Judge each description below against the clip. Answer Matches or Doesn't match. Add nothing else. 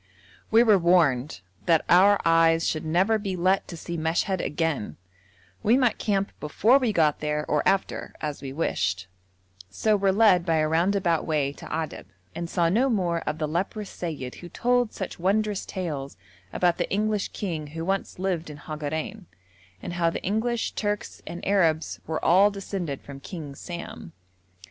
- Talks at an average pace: Matches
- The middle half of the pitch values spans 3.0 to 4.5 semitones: Matches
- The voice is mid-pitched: Matches